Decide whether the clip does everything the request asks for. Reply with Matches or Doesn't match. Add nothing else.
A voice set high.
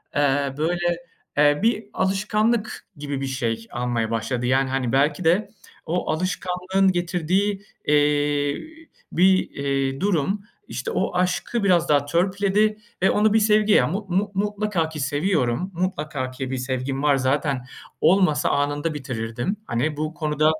Doesn't match